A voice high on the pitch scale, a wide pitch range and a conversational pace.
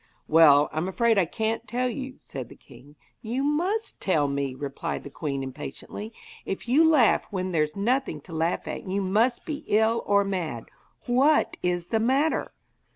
Yes: high, 200 Hz; wide, 8.2 semitones; average, 170 wpm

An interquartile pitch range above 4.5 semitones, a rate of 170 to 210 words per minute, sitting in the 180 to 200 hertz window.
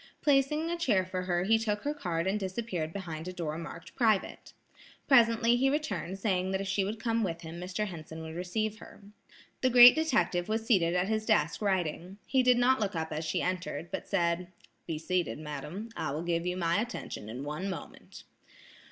Yes: average, 4.9 semitones; average, 200 wpm; high, 190 Hz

